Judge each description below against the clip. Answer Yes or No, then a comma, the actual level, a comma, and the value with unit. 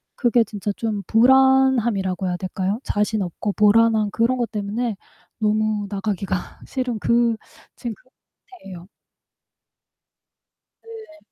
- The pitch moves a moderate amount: Yes, average, 3.0 semitones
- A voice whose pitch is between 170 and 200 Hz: No, high, 215 Hz